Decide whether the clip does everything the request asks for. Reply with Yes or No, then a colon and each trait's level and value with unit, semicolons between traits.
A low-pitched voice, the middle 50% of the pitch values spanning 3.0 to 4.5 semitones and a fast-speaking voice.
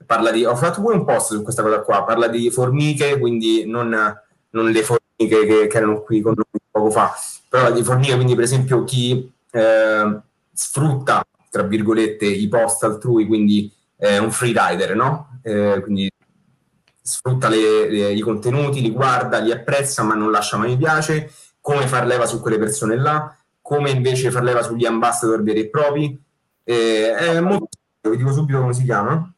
Yes: low, 120 Hz; average, 3.7 semitones; fast, 180 wpm